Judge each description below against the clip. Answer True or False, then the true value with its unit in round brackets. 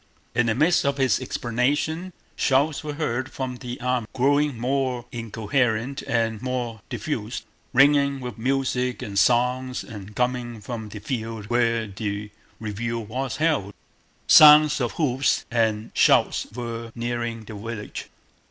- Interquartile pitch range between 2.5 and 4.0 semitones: True (3.1 semitones)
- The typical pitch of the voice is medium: False (120 Hz)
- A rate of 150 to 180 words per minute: False (135 wpm)